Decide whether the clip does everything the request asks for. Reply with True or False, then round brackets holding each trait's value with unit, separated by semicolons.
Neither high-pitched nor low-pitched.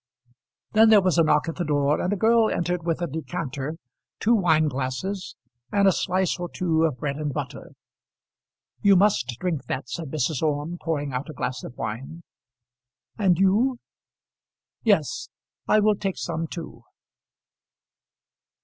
True (165 Hz)